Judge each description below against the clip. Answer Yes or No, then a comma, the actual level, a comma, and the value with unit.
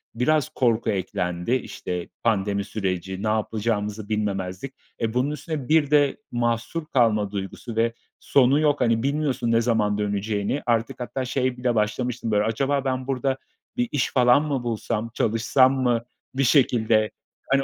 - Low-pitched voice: Yes, low, 115 Hz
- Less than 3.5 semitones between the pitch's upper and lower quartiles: No, average, 3.8 semitones